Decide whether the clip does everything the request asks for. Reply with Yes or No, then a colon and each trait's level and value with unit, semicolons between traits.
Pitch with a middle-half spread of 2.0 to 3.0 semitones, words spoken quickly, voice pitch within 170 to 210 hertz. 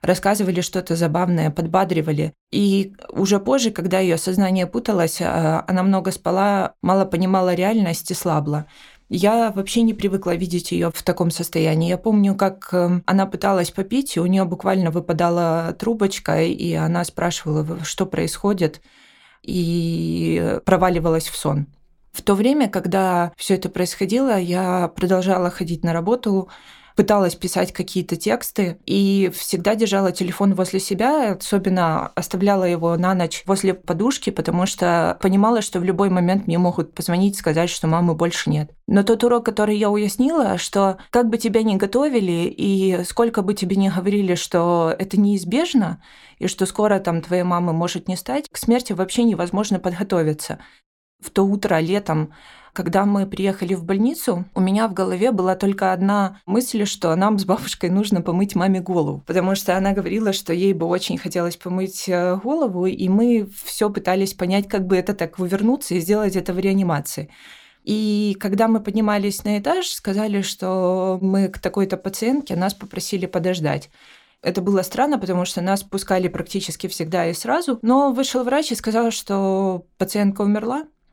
Yes: narrow, 2.6 semitones; fast, 160 wpm; high, 190 Hz